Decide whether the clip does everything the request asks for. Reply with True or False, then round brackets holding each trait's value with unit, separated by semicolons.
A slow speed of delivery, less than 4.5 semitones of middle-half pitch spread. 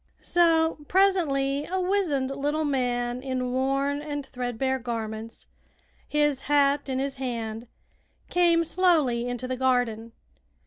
True (120 wpm; 3.3 semitones)